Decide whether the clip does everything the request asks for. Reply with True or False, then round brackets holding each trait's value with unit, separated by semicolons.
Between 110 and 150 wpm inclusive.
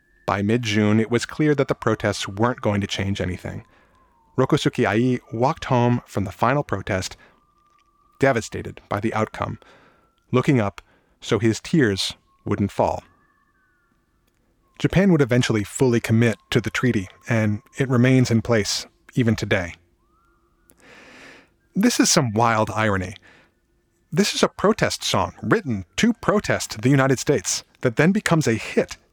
True (140 wpm)